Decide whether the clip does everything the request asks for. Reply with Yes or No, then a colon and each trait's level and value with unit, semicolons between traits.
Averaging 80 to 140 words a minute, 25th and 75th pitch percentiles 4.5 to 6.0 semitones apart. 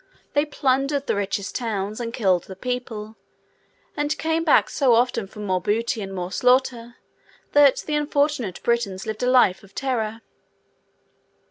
No: average, 150 wpm; average, 4.9 semitones